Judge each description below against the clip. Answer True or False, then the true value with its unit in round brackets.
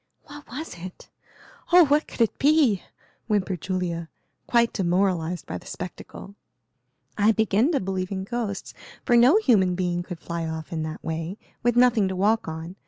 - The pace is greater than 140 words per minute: True (170 wpm)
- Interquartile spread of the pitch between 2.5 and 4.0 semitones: False (5.2 semitones)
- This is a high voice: True (195 Hz)